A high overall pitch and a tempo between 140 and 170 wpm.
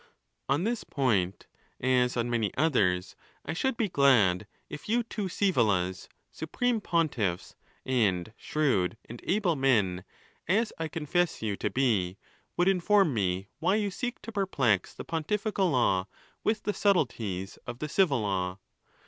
No: low, 135 Hz; average, 150 wpm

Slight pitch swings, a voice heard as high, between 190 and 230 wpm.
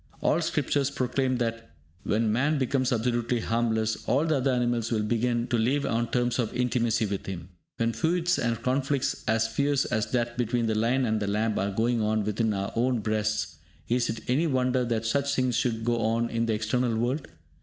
No: narrow, 2.3 semitones; low, 120 Hz; average, 195 wpm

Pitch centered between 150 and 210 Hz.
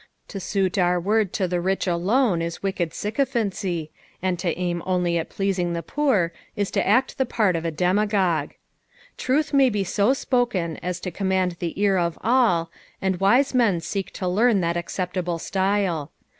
Yes: high, 190 Hz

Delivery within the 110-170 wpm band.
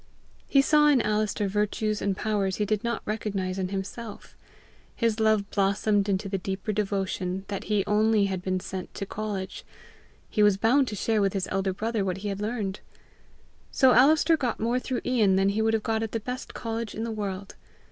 No: average, 200 wpm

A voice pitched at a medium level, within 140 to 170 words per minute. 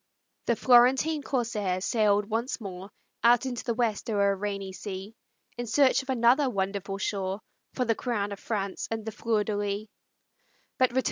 No: high, 215 Hz; average, 160 wpm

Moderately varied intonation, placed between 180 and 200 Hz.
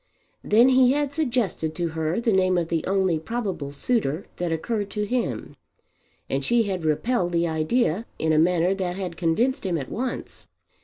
No: wide, 6.4 semitones; medium, 185 Hz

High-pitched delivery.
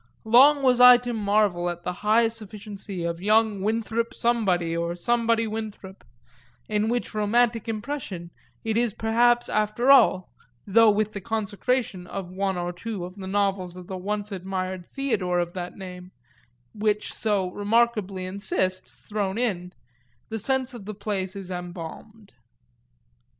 Yes: high, 205 Hz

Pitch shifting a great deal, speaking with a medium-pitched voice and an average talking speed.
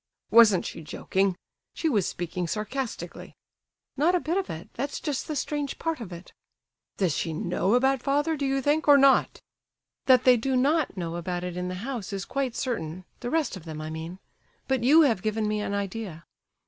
No: wide, 7.3 semitones; high, 230 Hz; average, 195 wpm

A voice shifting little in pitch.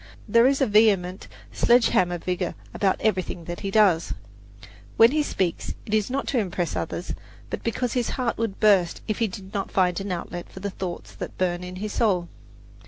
No: average, 3.9 semitones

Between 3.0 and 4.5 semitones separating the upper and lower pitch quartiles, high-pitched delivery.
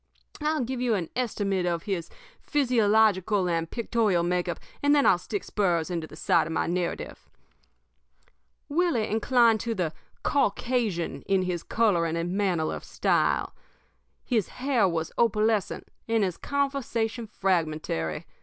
No: average, 5.2 semitones; high, 205 Hz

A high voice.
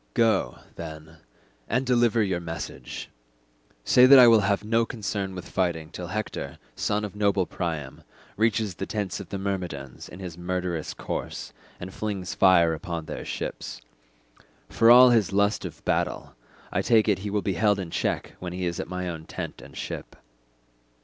No: very low, 95 Hz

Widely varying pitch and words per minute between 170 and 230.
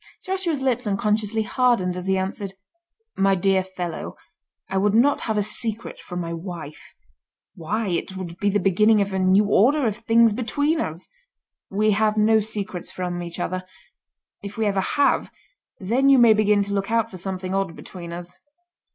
No: average, 3.2 semitones; average, 175 wpm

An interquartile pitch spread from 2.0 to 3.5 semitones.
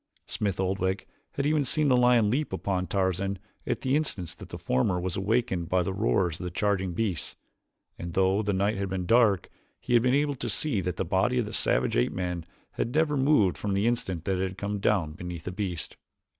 No: average, 4.4 semitones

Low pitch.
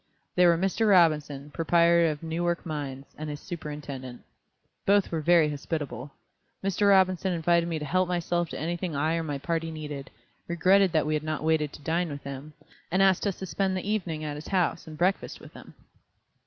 No: medium, 165 Hz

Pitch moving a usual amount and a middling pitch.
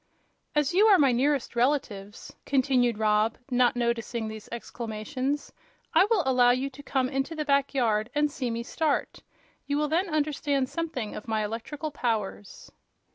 No: average, 4.1 semitones; very high, 260 Hz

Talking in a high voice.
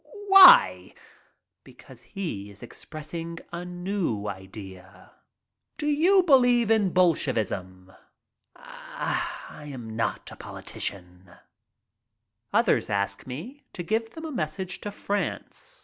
No: medium, 170 Hz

